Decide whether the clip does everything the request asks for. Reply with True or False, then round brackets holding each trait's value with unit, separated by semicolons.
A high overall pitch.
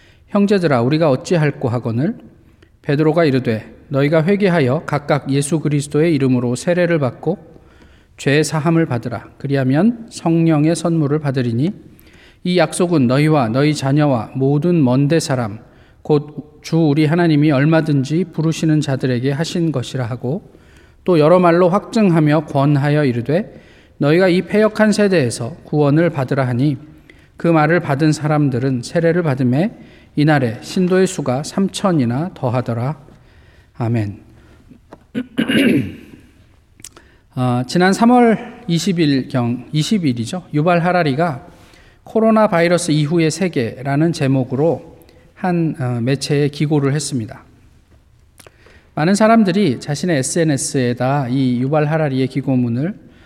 False (150 Hz)